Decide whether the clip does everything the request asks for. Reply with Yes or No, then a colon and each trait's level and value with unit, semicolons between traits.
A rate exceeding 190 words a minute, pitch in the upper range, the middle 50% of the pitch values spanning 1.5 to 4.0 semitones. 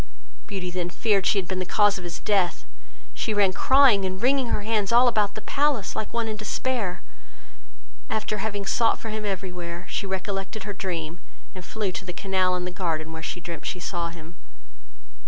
Yes: average, 200 wpm; high, 195 Hz; average, 3.2 semitones